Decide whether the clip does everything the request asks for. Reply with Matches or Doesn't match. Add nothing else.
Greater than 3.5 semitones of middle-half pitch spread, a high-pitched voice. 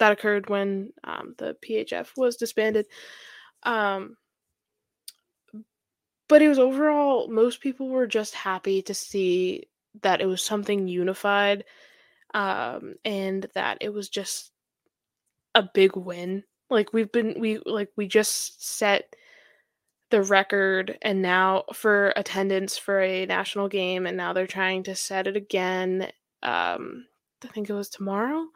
Doesn't match